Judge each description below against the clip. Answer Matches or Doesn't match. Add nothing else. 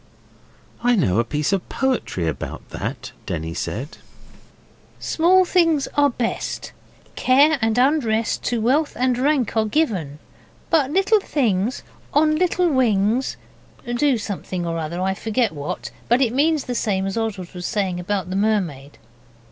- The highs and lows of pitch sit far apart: Matches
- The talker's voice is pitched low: Doesn't match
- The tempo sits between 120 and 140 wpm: Doesn't match